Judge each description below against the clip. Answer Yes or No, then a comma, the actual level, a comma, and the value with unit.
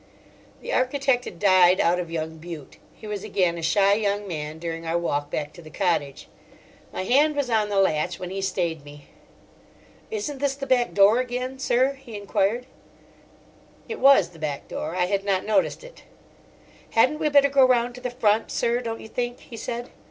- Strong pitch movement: Yes, wide, 6.6 semitones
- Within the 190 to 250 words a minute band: Yes, average, 195 wpm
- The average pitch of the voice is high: Yes, high, 205 Hz